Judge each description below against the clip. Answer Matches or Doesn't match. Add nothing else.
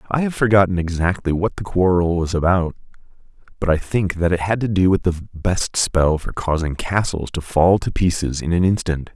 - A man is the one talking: Matches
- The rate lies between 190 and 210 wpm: Matches